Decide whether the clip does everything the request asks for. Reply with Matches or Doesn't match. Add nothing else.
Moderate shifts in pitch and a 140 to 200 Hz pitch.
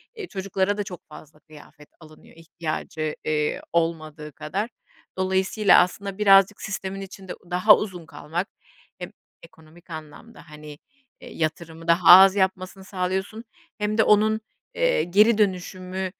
Matches